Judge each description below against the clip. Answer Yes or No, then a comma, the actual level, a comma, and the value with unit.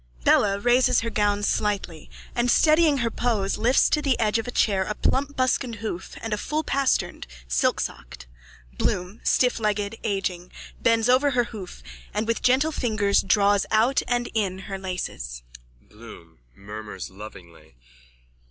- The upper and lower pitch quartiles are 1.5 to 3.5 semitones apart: No, average, 4.8 semitones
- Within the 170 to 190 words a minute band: No, average, 145 wpm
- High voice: Yes, high, 210 Hz